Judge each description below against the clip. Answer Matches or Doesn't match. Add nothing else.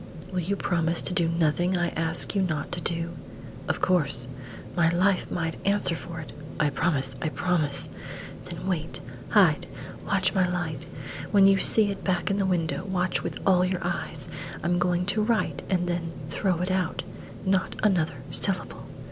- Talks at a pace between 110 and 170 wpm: Doesn't match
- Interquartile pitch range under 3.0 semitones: Matches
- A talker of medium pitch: Matches